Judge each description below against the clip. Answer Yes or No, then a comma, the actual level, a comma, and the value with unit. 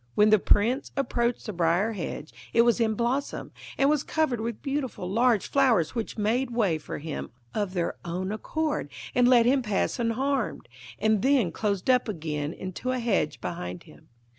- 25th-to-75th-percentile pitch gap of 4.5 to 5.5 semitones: Yes, average, 5.2 semitones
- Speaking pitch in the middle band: No, high, 225 Hz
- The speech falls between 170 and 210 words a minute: Yes, average, 175 wpm